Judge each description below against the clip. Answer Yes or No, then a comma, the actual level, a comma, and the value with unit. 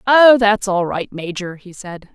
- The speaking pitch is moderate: No, high, 200 Hz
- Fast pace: No, average, 195 wpm